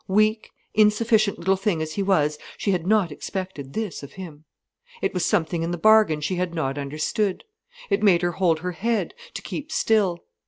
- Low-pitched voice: No, medium, 180 Hz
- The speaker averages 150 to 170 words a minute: No, average, 190 wpm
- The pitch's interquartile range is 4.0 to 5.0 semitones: Yes, average, 4.6 semitones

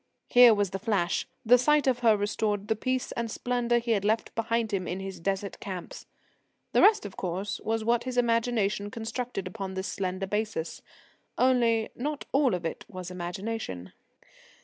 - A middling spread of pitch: Yes, average, 3.7 semitones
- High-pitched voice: Yes, high, 220 Hz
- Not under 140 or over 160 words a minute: No, average, 170 wpm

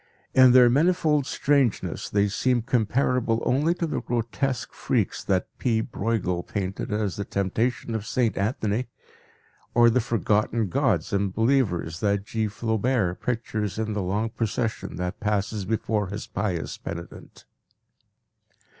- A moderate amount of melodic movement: Yes, average, 3.5 semitones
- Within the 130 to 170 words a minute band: Yes, slow, 135 wpm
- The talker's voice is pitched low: Yes, low, 110 Hz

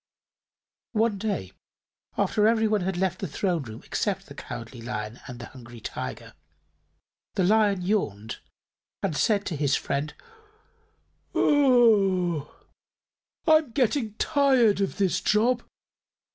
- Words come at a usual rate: No, slow, 115 wpm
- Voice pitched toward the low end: No, high, 190 Hz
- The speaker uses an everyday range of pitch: No, wide, 7.9 semitones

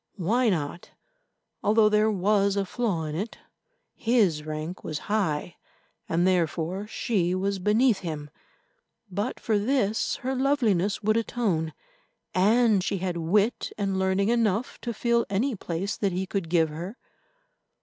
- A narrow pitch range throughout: No, average, 3.9 semitones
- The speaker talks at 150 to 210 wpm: No, average, 140 wpm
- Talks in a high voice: Yes, high, 195 Hz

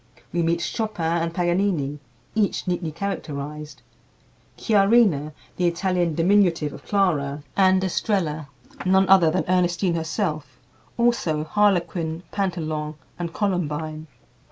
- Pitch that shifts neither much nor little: Yes, average, 3.6 semitones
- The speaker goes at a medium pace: No, slow, 105 wpm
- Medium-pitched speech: Yes, medium, 170 Hz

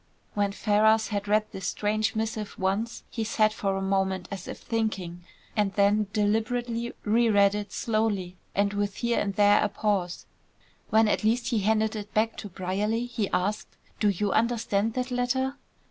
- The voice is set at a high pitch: Yes, high, 210 Hz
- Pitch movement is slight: Yes, narrow, 1.9 semitones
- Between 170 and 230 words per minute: Yes, average, 175 wpm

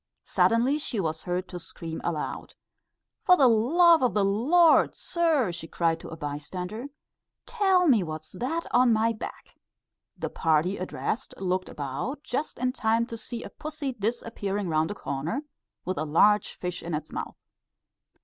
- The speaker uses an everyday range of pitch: No, wide, 7.4 semitones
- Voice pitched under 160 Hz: No, high, 210 Hz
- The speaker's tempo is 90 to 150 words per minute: No, average, 160 wpm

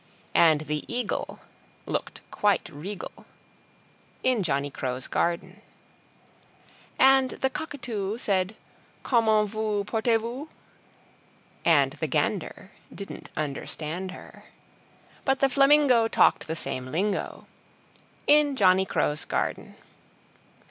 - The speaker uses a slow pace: Yes, slow, 100 wpm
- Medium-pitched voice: No, high, 210 Hz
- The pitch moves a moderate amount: No, wide, 6.4 semitones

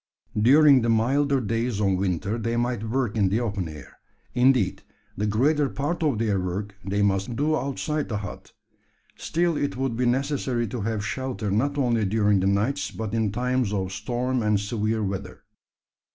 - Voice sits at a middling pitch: No, low, 115 Hz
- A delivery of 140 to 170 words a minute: No, average, 180 wpm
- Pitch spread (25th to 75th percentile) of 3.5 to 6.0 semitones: Yes, average, 4.2 semitones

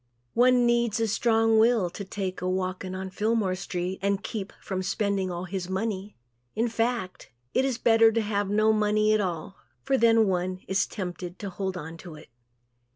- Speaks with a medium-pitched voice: No, high, 200 Hz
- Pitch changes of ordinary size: Yes, average, 3.3 semitones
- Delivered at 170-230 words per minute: Yes, average, 185 wpm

